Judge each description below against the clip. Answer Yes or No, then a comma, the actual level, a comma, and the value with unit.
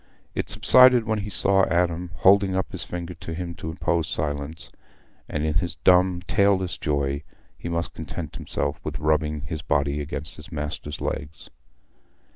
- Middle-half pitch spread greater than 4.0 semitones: No, average, 3.2 semitones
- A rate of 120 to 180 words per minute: Yes, average, 160 wpm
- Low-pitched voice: Yes, very low, 85 Hz